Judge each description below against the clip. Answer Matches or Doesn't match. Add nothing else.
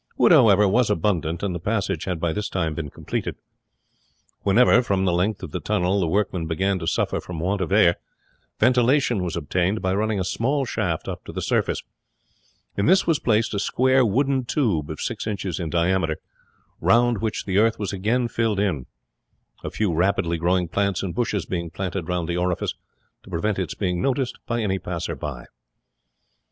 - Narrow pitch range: Doesn't match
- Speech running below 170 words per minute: Doesn't match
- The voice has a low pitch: Matches